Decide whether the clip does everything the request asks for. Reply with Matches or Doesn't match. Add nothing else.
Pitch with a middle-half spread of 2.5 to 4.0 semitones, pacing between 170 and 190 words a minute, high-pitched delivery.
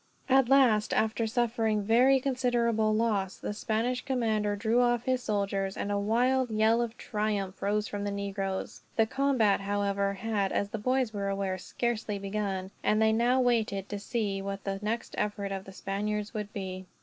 Matches